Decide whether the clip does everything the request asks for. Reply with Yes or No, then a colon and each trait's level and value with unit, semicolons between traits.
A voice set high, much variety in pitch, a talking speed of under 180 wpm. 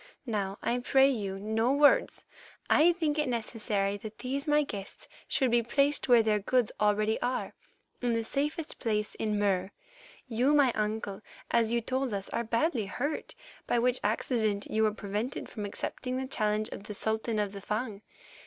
No: high, 225 Hz; average, 3.6 semitones; average, 170 wpm